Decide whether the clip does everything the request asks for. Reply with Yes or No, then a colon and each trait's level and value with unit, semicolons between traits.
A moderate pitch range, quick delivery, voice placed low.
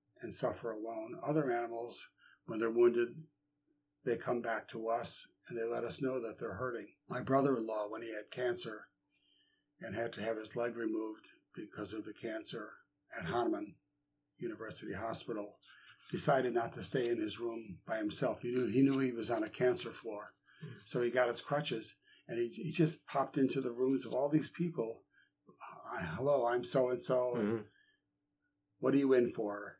No: average, 4.1 semitones; average, 180 wpm; low, 125 Hz